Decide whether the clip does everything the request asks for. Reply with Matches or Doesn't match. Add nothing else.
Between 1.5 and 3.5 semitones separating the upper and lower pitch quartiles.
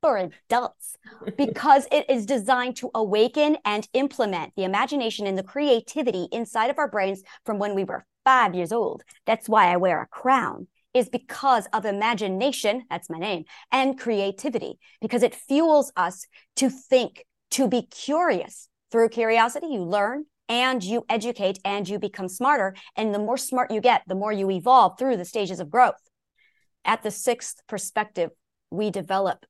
Doesn't match